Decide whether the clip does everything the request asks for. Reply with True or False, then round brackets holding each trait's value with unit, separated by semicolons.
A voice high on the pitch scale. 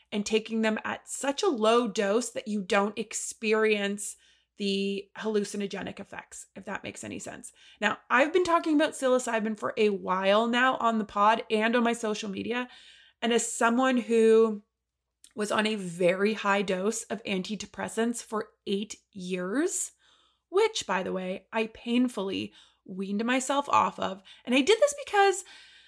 True (225 Hz)